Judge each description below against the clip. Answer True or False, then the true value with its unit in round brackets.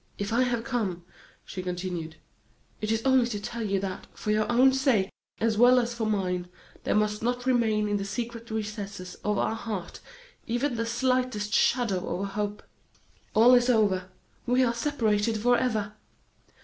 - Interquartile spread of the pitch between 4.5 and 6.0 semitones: False (3.1 semitones)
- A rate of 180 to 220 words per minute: False (170 wpm)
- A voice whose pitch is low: False (220 Hz)